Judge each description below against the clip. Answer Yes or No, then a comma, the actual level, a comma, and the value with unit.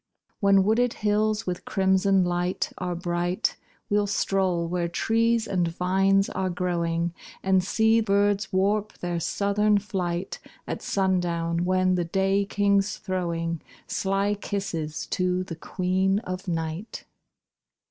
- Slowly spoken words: Yes, slow, 125 wpm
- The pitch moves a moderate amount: No, narrow, 2.3 semitones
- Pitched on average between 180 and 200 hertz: Yes, high, 190 Hz